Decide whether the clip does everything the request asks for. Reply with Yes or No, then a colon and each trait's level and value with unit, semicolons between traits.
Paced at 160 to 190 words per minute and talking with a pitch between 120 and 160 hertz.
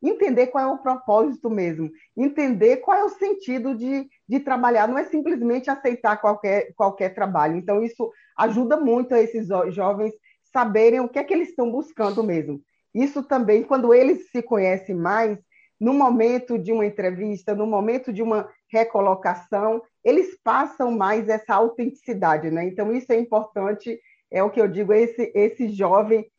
No: average, 165 wpm; high, 225 Hz